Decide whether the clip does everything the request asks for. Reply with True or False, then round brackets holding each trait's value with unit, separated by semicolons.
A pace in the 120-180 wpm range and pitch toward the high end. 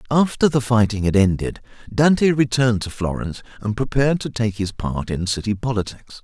False (175 wpm; 115 Hz)